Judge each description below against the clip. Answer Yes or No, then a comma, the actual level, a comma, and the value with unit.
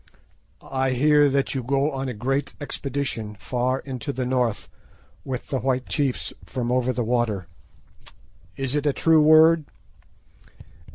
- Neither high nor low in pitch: No, low, 130 Hz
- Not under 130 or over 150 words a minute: Yes, average, 145 wpm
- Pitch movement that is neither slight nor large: No, narrow, 2.3 semitones